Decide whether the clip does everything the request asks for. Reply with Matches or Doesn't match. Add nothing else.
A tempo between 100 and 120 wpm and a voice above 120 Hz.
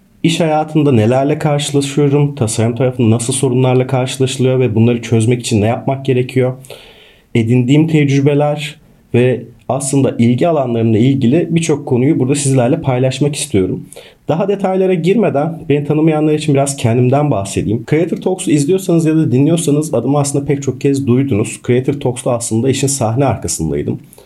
Doesn't match